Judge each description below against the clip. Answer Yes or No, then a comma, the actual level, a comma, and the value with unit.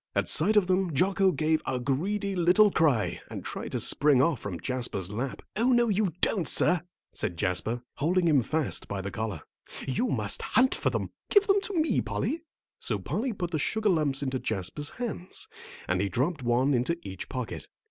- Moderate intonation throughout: No, wide, 8.0 semitones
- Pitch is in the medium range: Yes, medium, 155 Hz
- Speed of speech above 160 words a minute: Yes, average, 190 wpm